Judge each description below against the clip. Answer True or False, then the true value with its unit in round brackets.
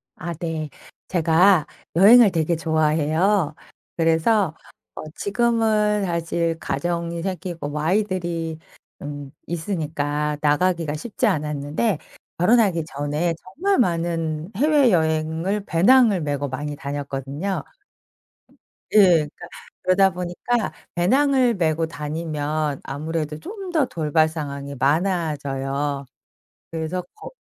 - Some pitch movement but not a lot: True (4.2 semitones)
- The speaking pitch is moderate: True (165 Hz)